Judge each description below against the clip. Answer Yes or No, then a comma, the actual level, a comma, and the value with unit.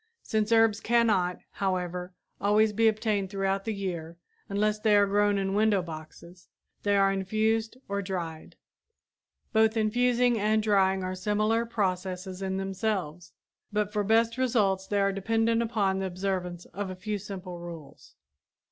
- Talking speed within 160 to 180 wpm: No, average, 145 wpm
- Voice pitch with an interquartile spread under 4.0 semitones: Yes, average, 2.7 semitones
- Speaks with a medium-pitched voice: No, high, 200 Hz